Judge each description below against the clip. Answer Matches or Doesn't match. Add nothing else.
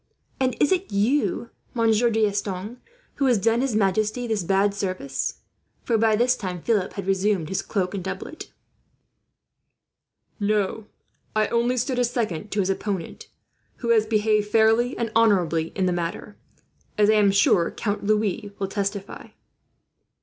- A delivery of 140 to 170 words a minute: Matches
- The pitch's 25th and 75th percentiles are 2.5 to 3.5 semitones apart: Matches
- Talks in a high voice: Matches